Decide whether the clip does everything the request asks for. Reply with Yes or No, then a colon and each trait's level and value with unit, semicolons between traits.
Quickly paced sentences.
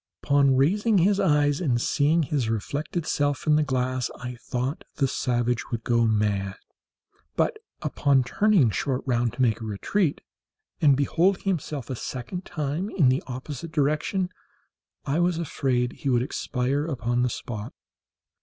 No: average, 155 wpm